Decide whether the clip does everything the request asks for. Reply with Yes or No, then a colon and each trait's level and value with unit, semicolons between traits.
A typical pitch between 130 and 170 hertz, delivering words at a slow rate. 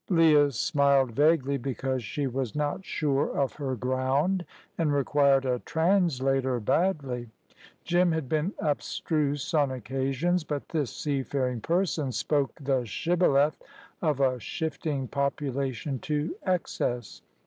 Yes: medium, 140 Hz; slow, 120 wpm